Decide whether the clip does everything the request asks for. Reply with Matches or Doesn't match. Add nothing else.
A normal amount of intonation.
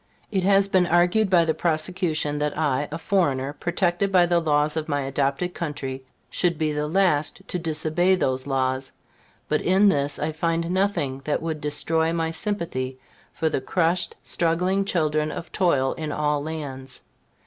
Matches